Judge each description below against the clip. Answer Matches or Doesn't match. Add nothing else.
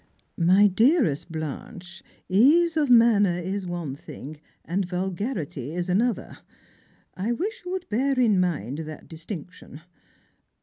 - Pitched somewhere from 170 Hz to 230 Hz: Matches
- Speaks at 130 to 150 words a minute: Matches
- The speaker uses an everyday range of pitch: Doesn't match